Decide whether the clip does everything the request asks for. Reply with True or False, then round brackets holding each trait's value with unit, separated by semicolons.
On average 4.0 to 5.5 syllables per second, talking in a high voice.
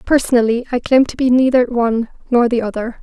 False (6.0 syllables/s; 240 Hz)